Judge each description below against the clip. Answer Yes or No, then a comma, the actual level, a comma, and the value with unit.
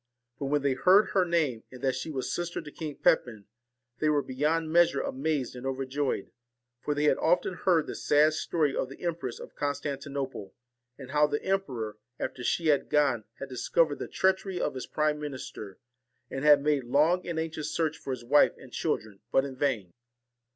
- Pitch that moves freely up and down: No, average, 3.4 semitones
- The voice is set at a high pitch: No, medium, 145 Hz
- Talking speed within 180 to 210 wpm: Yes, average, 190 wpm